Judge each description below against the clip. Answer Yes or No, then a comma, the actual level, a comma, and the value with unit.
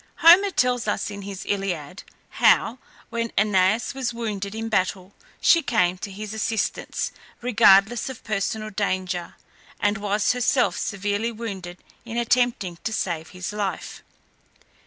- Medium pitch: No, high, 210 Hz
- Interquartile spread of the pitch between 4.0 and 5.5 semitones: No, average, 3.4 semitones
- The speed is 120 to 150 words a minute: Yes, slow, 135 wpm